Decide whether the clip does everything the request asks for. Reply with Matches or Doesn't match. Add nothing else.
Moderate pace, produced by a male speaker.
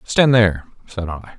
Matches